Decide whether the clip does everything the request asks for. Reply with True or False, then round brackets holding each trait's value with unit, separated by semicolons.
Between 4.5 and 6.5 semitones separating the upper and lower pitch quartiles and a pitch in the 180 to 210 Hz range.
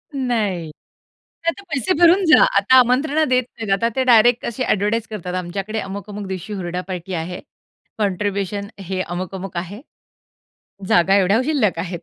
True (4.8 semitones; 205 Hz)